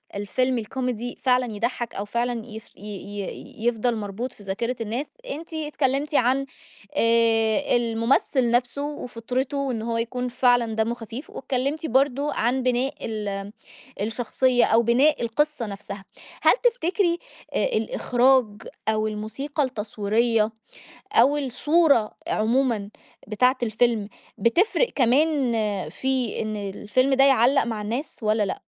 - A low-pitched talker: No, high, 240 Hz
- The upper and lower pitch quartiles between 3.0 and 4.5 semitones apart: Yes, average, 3.4 semitones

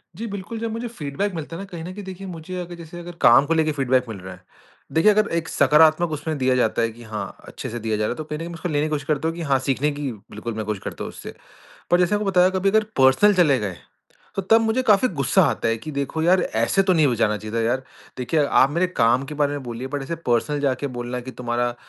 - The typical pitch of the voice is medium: Yes, medium, 150 Hz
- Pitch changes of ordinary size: No, wide, 6.2 semitones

